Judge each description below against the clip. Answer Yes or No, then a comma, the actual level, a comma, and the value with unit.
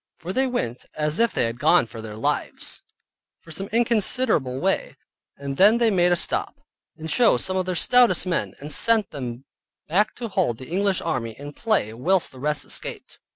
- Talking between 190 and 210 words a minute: Yes, average, 195 wpm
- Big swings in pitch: Yes, wide, 8.1 semitones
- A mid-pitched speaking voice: Yes, medium, 175 Hz